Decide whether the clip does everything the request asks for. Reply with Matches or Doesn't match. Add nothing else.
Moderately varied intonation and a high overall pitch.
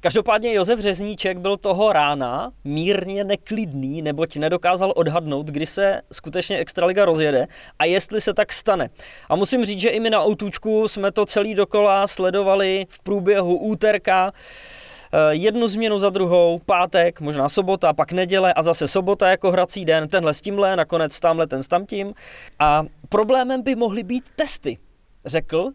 Matches